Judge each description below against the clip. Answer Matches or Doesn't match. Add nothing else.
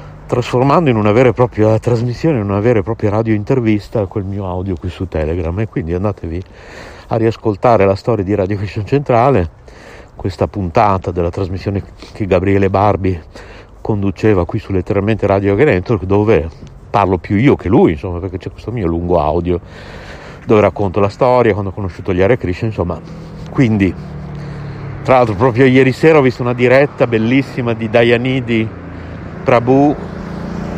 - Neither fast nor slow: Matches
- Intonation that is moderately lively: Matches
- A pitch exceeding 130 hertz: Doesn't match